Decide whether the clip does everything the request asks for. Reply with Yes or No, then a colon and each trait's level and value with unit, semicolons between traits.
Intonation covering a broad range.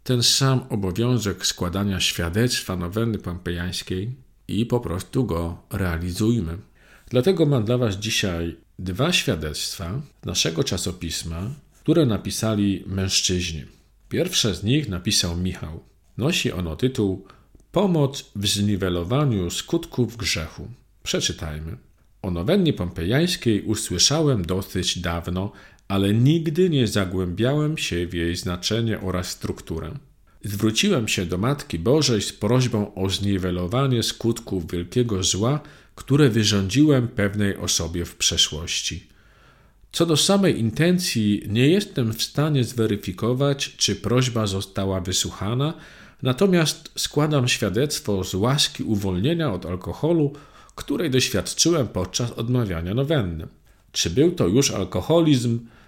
Yes: wide, 5.9 semitones